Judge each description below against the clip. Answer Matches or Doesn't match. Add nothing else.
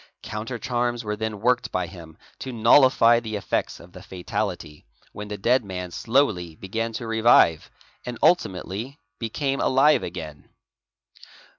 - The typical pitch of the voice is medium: Doesn't match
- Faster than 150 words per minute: Doesn't match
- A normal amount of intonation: Matches